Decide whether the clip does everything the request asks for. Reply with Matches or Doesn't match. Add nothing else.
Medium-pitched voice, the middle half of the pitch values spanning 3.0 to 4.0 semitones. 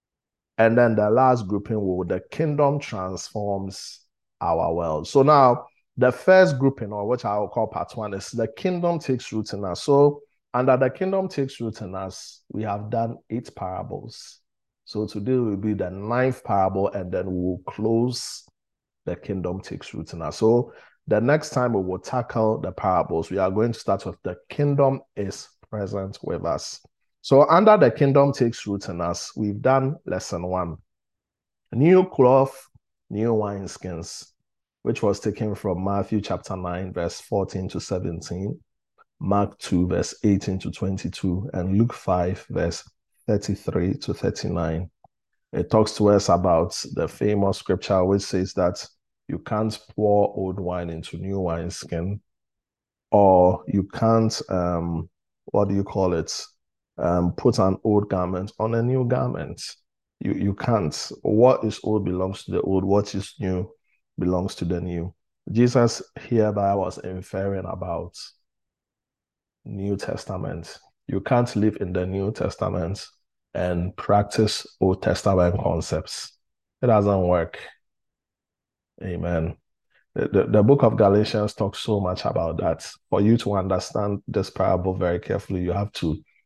Doesn't match